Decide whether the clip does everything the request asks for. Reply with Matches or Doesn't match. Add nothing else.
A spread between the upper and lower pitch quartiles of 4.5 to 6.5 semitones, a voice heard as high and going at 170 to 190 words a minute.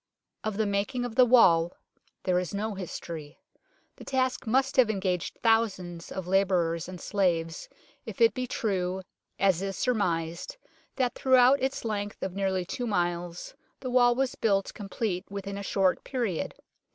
Doesn't match